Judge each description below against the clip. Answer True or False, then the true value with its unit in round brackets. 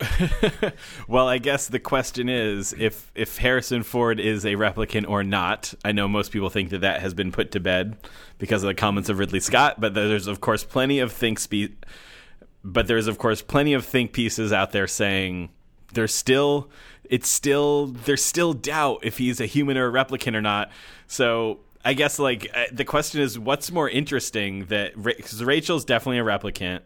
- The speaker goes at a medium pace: True (190 wpm)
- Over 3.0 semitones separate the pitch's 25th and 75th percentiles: True (4.2 semitones)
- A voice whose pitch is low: True (110 Hz)